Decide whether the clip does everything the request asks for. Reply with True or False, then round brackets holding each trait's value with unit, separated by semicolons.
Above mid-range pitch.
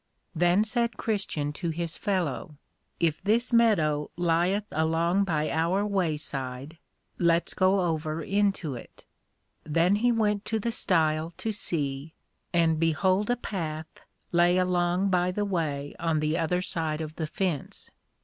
False (170 Hz)